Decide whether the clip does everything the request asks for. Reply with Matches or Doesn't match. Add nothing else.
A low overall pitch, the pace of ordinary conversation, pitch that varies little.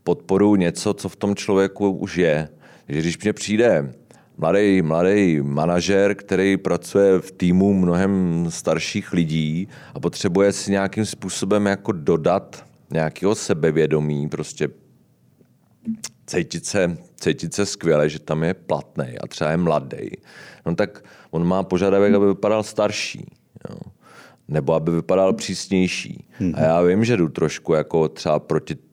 Doesn't match